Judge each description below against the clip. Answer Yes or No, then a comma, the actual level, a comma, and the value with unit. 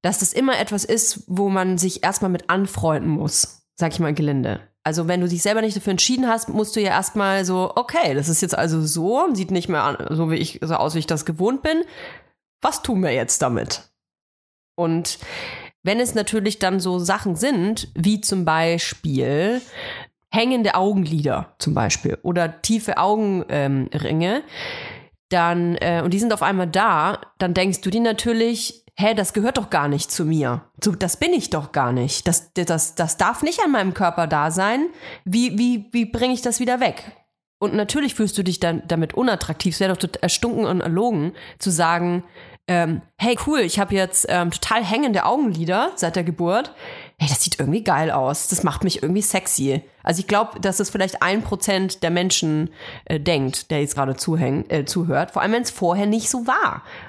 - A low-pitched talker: No, medium, 185 Hz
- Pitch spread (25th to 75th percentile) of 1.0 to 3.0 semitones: No, average, 4.5 semitones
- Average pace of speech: No, fast, 195 wpm